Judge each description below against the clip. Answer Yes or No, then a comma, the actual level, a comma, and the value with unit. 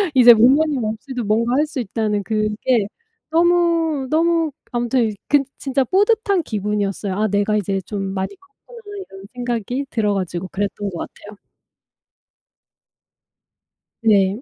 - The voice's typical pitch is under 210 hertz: No, high, 230 Hz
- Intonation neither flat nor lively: No, wide, 6.4 semitones